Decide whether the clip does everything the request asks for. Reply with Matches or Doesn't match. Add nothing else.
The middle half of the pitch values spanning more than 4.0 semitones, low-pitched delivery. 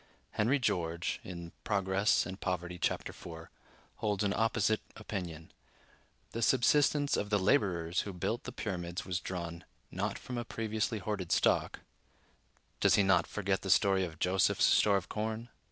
Doesn't match